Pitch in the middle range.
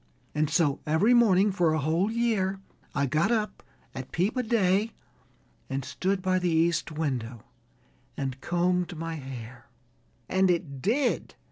Yes: medium, 175 Hz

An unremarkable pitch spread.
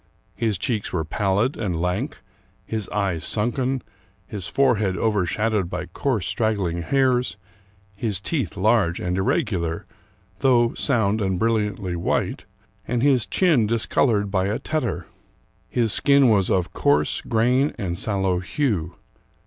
Yes: average, 4.6 semitones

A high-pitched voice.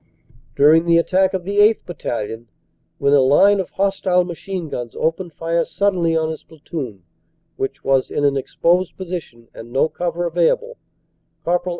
No: medium, 170 Hz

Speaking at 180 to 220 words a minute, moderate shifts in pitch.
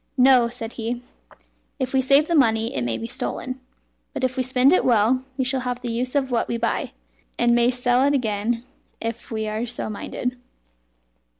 No: average, 195 wpm; narrow, 2.1 semitones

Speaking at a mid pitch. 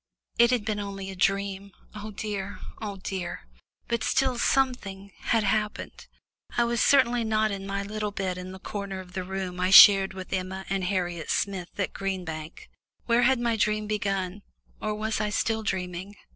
No: high, 200 Hz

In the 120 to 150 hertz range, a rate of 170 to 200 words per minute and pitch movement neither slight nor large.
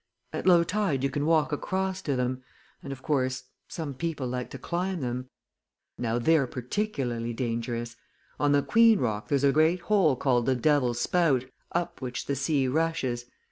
Yes: medium, 140 Hz; average, 175 wpm; average, 4.7 semitones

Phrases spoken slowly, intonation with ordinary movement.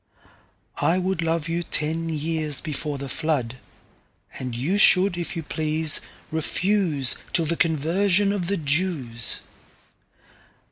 Yes: slow, 105 wpm; average, 3.0 semitones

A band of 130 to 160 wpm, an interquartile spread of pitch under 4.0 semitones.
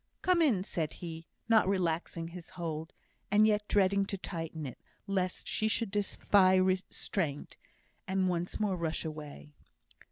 Yes: average, 140 wpm; average, 3.4 semitones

